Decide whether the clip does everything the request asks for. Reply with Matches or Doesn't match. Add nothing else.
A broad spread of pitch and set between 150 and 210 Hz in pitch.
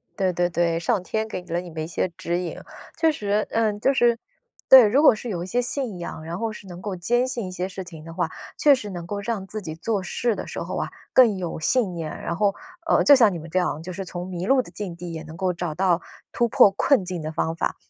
Doesn't match